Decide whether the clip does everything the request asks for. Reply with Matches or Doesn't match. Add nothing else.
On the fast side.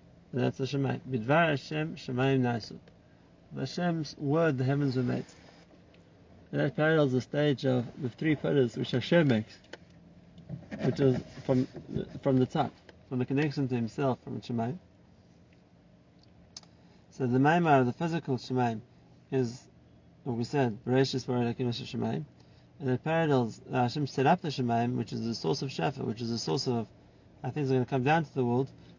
Doesn't match